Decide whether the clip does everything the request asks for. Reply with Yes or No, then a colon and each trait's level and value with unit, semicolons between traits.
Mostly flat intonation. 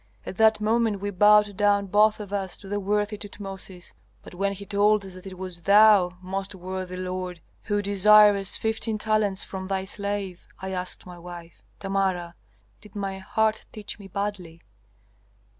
Yes: narrow, 1.9 semitones